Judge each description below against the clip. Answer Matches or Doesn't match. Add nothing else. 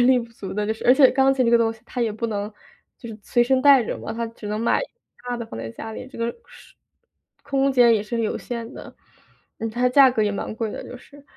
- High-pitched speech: Matches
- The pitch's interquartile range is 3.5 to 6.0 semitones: Doesn't match